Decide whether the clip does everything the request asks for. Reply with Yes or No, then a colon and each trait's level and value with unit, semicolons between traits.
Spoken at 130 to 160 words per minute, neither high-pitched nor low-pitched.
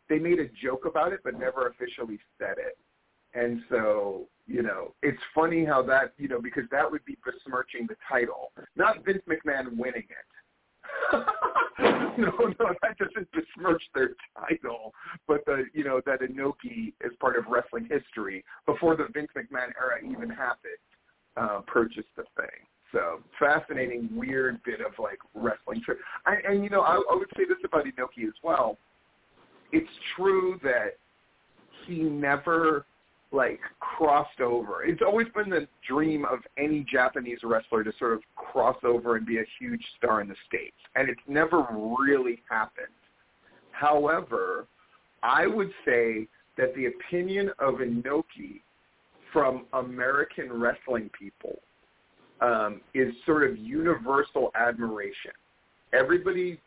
Yes: average, 145 wpm; medium, 165 Hz